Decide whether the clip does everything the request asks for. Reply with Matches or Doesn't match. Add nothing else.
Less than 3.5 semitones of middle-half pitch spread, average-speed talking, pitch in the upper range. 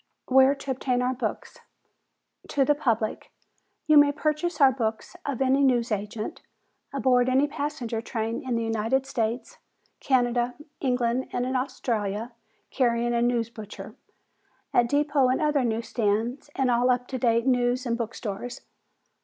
Matches